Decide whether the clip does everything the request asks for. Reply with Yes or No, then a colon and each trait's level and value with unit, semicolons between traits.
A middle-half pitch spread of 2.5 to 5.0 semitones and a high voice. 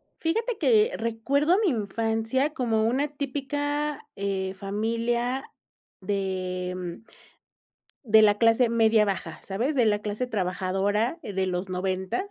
No: wide, 5.4 semitones; high, 225 Hz